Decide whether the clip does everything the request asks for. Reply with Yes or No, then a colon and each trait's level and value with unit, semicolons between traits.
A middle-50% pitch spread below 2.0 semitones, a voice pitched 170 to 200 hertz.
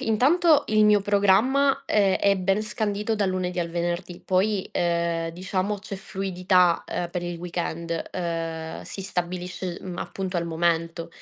No: average, 2.9 semitones; medium, 185 Hz